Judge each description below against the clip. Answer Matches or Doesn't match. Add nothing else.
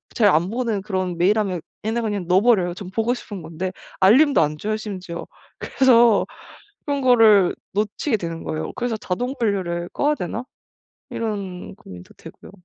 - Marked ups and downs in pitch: Doesn't match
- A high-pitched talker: Matches